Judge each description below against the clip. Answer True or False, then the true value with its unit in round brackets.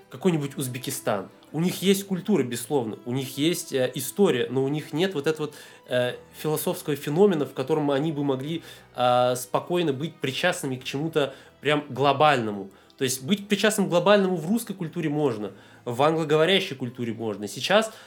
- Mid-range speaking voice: True (150 Hz)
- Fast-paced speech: True (165 wpm)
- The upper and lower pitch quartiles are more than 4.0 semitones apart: True (5.2 semitones)